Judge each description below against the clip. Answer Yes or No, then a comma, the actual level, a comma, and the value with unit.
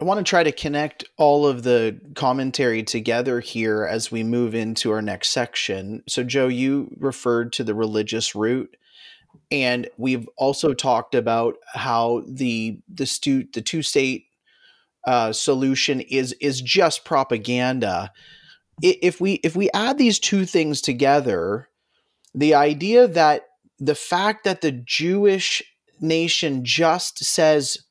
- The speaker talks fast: No, average, 140 wpm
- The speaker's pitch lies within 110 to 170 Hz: Yes, low, 135 Hz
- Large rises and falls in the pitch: No, average, 4.9 semitones